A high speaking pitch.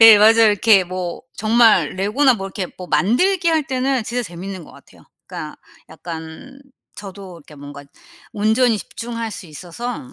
Yes: high, 210 Hz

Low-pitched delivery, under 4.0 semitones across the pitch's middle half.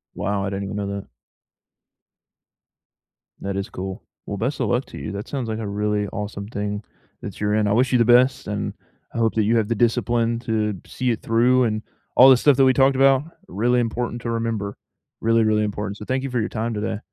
Yes: low, 110 Hz; average, 2.9 semitones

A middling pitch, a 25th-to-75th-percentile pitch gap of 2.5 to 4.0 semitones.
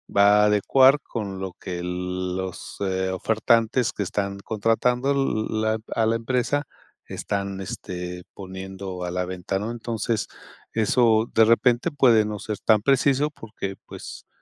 No: low, 105 Hz; average, 3.6 semitones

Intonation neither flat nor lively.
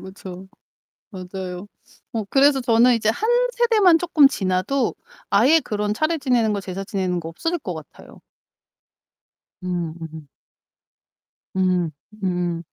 No: wide, 7.0 semitones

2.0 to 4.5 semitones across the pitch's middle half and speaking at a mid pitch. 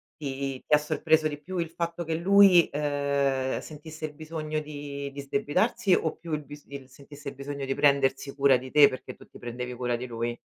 Yes: narrow, 2.5 semitones; medium, 145 Hz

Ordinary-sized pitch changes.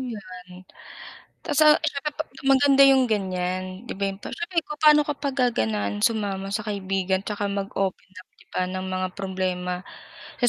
No: wide, 6.0 semitones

